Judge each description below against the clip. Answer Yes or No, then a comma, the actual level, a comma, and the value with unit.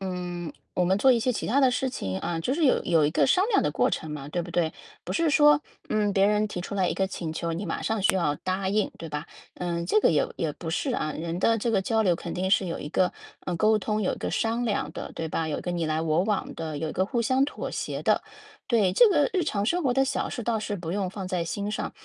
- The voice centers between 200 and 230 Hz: No, high, 190 Hz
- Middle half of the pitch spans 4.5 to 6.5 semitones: Yes, average, 5.0 semitones